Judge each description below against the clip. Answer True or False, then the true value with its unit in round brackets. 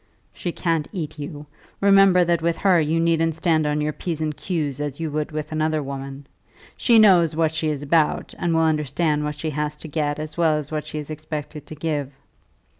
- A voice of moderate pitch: True (155 Hz)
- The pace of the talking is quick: True (210 wpm)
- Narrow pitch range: True (1.8 semitones)